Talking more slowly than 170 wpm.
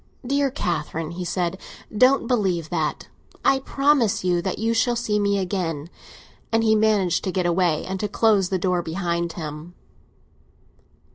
Yes: average, 155 wpm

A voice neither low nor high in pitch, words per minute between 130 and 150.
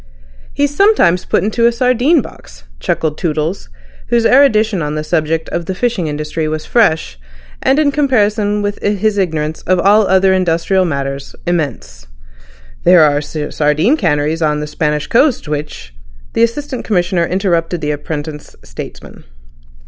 Yes: medium, 175 Hz; average, 145 wpm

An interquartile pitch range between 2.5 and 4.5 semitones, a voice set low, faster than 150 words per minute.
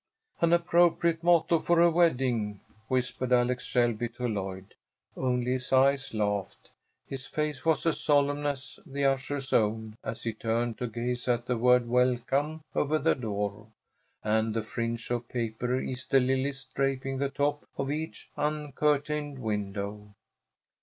No: average, 3.7 semitones; low, 125 Hz; average, 145 wpm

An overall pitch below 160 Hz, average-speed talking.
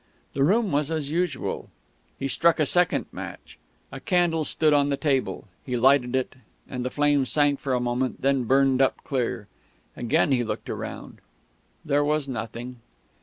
Yes: medium, 140 Hz; average, 170 wpm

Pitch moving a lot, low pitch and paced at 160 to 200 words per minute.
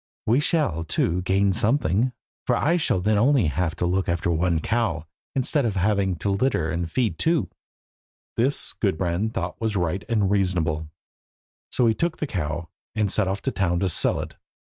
No: average, 4.9 semitones; very low, 95 Hz; average, 180 wpm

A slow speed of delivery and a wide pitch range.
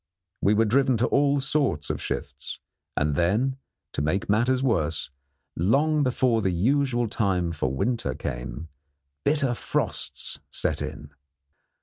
Yes: slow, 130 wpm; wide, 7.8 semitones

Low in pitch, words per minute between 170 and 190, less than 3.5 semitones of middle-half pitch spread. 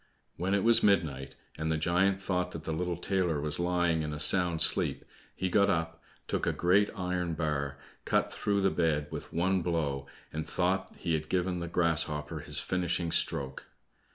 Yes: very low, 85 Hz; average, 180 wpm; average, 2.8 semitones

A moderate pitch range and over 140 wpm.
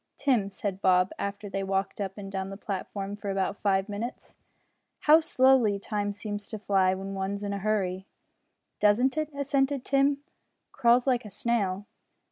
Yes: average, 3.7 semitones; average, 170 wpm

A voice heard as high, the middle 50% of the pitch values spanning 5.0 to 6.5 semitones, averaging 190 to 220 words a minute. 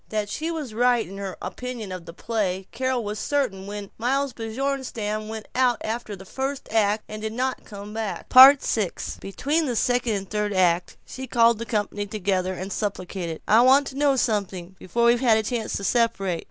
No: high, 220 Hz; average, 3.9 semitones; average, 195 wpm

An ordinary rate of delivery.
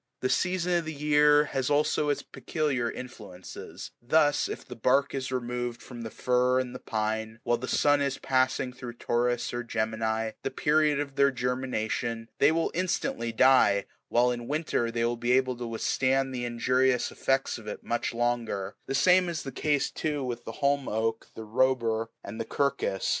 Yes: average, 180 wpm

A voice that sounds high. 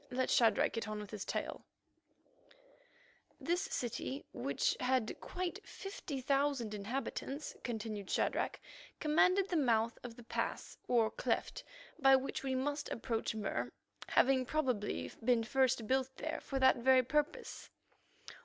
Yes: very high, 260 Hz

